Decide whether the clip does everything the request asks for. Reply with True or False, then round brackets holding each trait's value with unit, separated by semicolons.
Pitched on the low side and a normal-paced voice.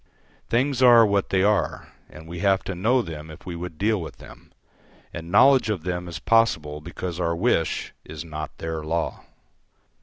True (90 Hz; 180 wpm)